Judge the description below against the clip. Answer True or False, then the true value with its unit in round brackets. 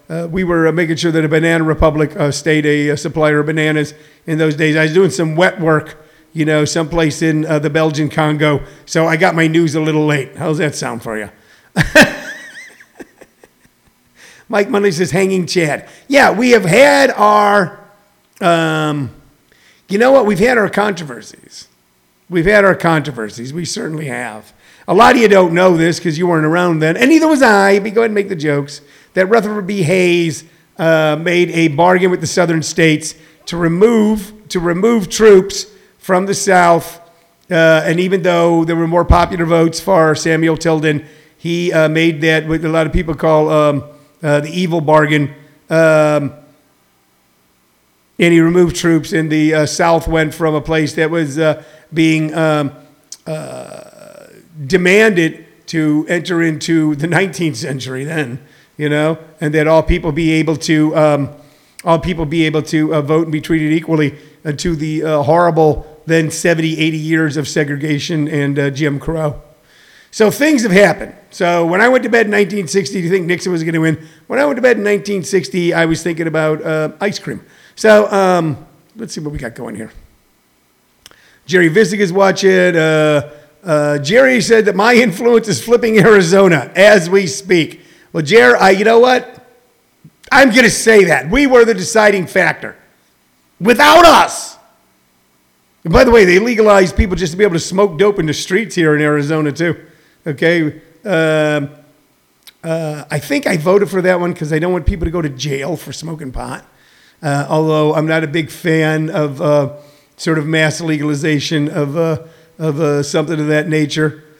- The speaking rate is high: False (180 wpm)